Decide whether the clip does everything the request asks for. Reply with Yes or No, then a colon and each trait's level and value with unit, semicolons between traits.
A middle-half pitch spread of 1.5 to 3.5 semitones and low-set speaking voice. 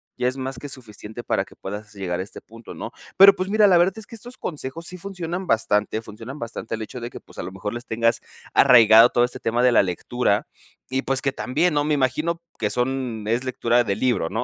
No: average, 5.0 semitones; low, 125 Hz